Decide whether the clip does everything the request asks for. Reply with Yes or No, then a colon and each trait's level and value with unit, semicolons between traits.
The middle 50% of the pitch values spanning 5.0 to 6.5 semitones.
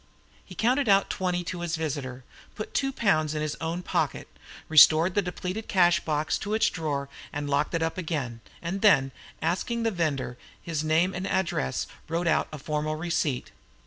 No: average, 3.4 semitones